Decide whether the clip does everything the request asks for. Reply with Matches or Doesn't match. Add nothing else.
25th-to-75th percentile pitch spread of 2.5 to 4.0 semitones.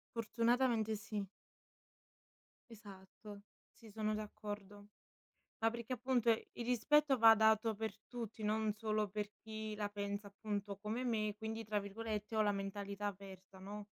Doesn't match